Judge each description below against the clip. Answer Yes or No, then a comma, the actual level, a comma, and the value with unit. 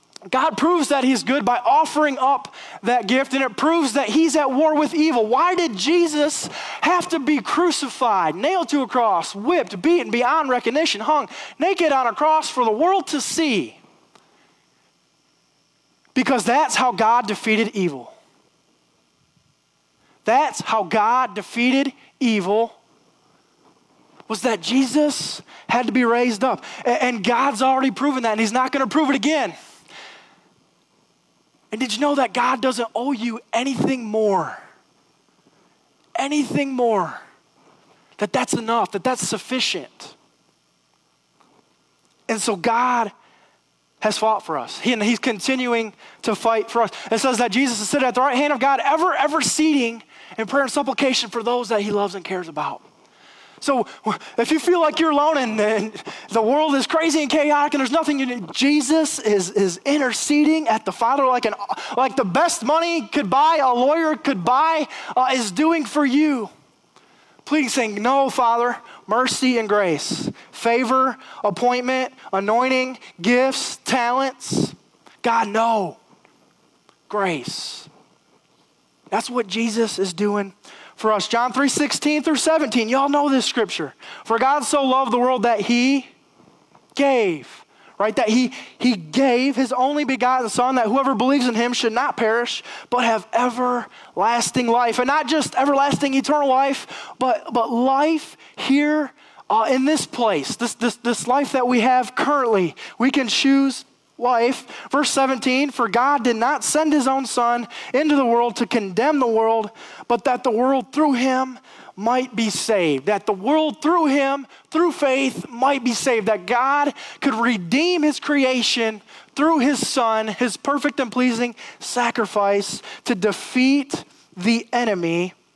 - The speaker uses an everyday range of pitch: Yes, average, 3.6 semitones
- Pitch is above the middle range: Yes, very high, 255 Hz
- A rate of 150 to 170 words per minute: Yes, average, 155 wpm